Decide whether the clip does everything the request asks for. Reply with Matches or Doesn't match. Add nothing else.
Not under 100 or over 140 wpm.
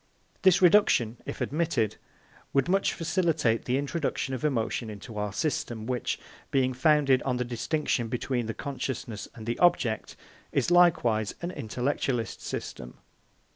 Matches